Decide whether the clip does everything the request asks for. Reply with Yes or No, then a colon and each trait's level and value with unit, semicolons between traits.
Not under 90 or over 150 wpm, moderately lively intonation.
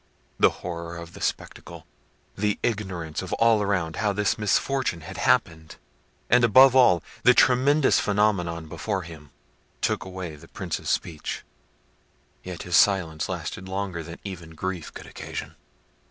Yes: average, 140 wpm; average, 4.0 semitones